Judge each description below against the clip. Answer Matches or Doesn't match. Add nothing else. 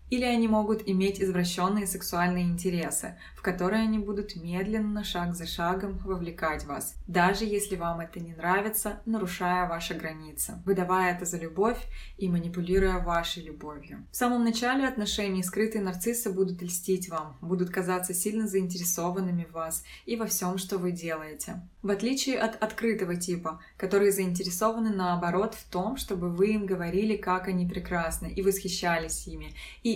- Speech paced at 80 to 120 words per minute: Doesn't match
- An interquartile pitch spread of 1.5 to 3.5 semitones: Matches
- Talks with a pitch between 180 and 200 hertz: Matches